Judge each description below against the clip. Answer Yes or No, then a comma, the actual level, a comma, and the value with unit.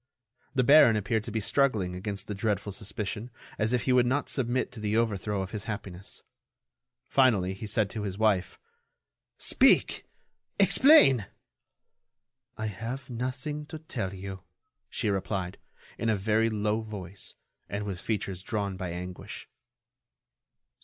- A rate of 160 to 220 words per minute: No, average, 140 wpm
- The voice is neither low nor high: No, low, 105 Hz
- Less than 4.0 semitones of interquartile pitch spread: Yes, average, 3.4 semitones